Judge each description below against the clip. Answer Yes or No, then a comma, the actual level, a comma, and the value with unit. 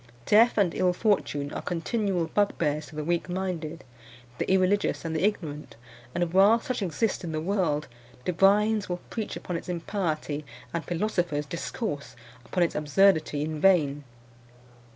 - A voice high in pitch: No, medium, 175 Hz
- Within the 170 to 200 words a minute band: No, average, 150 wpm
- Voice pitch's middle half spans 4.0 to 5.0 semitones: Yes, average, 4.3 semitones